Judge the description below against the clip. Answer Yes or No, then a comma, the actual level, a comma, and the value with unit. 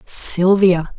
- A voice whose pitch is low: No, medium, 180 Hz